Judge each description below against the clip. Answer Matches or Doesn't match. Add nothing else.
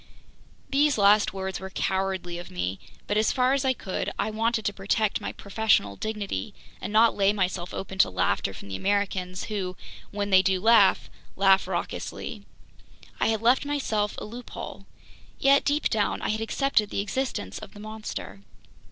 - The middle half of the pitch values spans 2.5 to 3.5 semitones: Matches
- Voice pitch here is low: Doesn't match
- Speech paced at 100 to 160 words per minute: Doesn't match